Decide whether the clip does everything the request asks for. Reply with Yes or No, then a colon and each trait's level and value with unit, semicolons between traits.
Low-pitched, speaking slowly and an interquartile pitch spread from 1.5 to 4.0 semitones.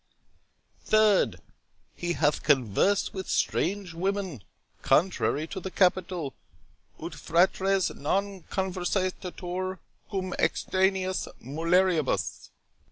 No: medium, 185 Hz; slow, 85 wpm; narrow, 2.6 semitones